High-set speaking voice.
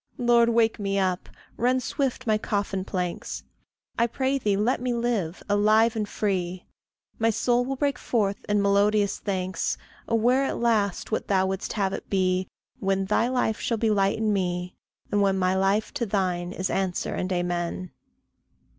Yes: high, 205 Hz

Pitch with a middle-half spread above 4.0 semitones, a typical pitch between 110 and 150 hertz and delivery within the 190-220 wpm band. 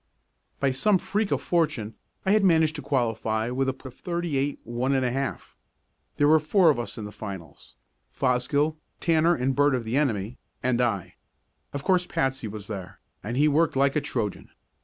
Yes: average, 4.7 semitones; low, 135 Hz; average, 195 wpm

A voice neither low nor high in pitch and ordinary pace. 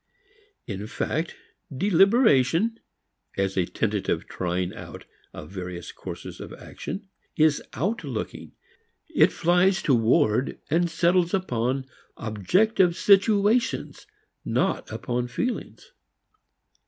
No: medium, 160 Hz; slow, 90 wpm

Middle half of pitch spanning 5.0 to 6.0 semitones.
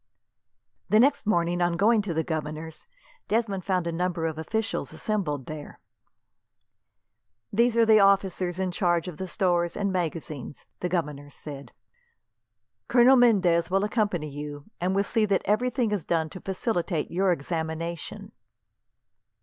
No: average, 4.2 semitones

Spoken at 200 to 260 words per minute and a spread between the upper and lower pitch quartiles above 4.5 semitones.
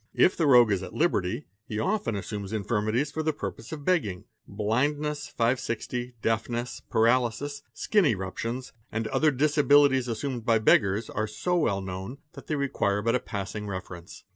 No: average, 165 wpm; wide, 5.5 semitones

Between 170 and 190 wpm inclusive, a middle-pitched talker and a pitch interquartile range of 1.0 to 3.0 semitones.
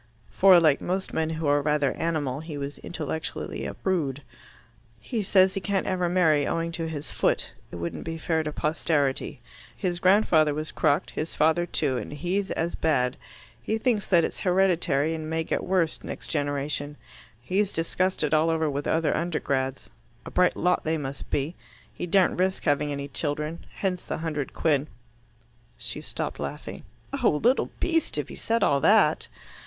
No: average, 175 wpm; medium, 160 Hz; average, 3.7 semitones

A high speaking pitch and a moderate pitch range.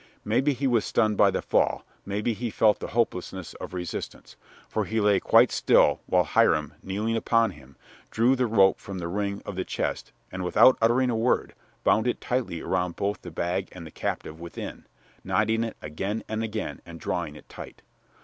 No: low, 105 Hz; average, 4.0 semitones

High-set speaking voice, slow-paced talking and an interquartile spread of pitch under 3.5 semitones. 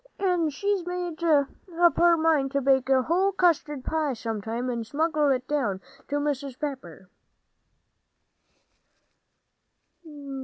No: very high, 290 Hz; slow, 115 wpm; average, 4.4 semitones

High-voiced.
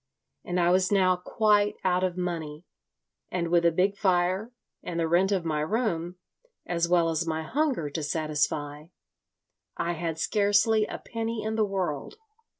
No: medium, 180 Hz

